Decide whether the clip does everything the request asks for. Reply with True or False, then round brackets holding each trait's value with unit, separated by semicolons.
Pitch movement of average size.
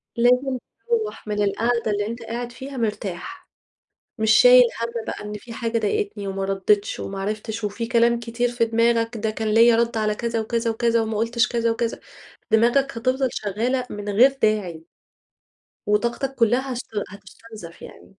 False (2.2 semitones)